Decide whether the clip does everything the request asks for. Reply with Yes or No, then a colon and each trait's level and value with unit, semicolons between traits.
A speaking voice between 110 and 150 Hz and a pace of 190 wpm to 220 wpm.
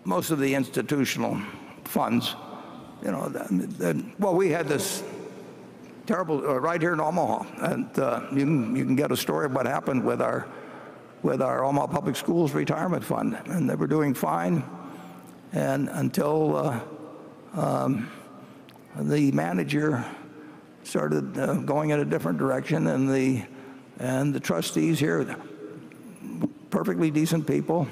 No: low, 135 Hz; average, 145 wpm